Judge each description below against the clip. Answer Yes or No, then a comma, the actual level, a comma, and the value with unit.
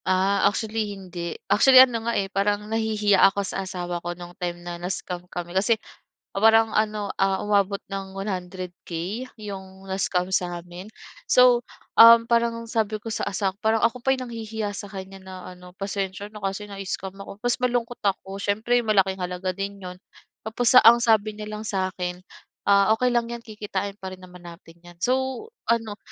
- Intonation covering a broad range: No, average, 2.9 semitones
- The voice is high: Yes, high, 200 Hz